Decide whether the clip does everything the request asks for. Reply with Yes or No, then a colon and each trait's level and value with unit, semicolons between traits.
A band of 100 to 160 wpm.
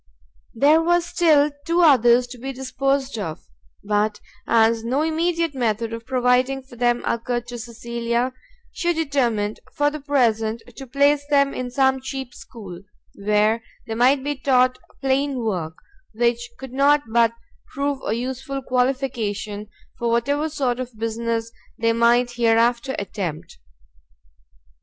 Yes: average, 140 wpm